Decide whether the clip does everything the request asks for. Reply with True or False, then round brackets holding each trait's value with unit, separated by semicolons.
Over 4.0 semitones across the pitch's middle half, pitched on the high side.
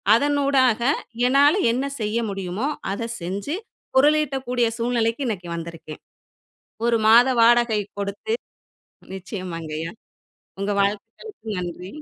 True (5.1 semitones; 230 Hz)